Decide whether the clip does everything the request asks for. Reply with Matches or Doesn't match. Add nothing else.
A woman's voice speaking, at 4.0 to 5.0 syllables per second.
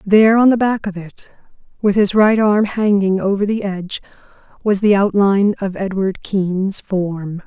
Matches